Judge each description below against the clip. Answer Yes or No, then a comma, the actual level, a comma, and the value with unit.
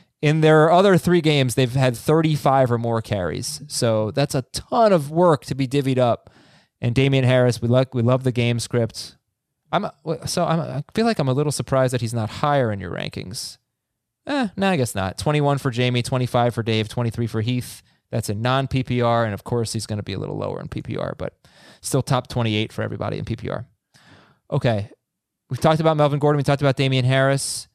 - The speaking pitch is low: Yes, low, 130 Hz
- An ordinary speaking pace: No, fast, 215 wpm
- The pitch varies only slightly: No, average, 3.7 semitones